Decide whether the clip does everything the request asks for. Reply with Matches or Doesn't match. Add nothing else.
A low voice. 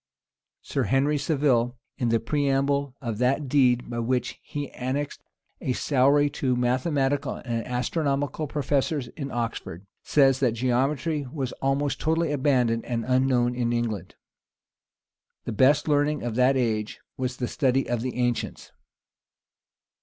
Matches